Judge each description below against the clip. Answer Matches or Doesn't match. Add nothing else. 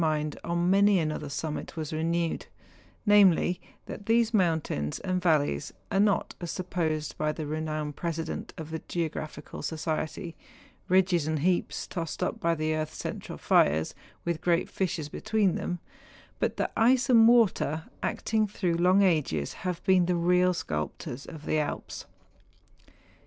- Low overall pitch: Doesn't match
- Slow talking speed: Doesn't match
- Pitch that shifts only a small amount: Doesn't match